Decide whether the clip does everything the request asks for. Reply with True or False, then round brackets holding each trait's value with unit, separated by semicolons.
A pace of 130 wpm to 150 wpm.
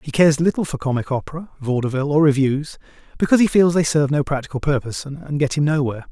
False (205 wpm)